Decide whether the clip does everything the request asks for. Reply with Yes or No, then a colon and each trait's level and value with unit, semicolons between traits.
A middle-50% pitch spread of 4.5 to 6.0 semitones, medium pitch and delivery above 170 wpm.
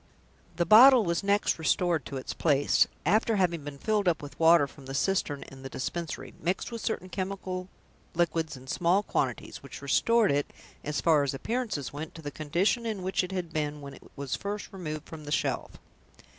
Yes: average, 4.9 semitones; medium, 170 Hz; average, 195 wpm